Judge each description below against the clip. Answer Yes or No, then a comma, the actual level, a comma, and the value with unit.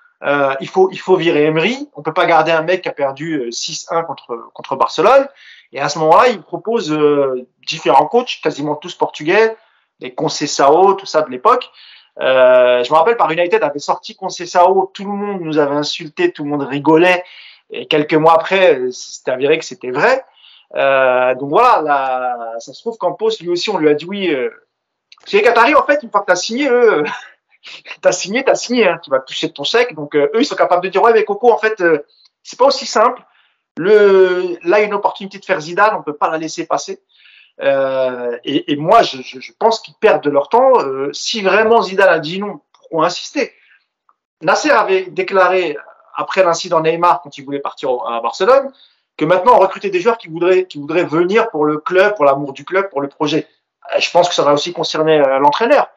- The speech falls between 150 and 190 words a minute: No, fast, 220 wpm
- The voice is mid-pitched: Yes, medium, 175 Hz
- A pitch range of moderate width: No, wide, 6.4 semitones